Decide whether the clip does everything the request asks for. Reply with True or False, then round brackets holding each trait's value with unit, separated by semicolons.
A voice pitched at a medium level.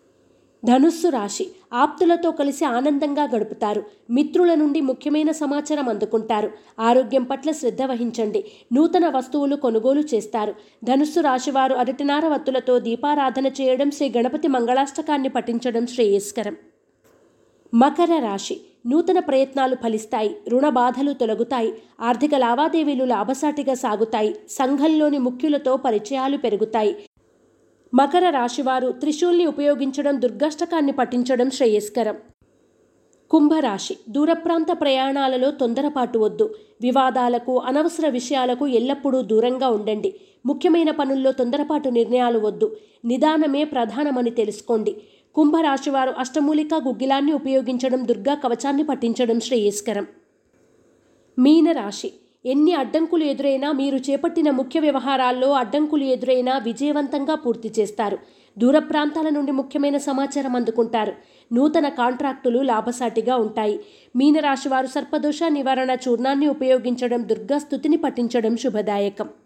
False (265 Hz)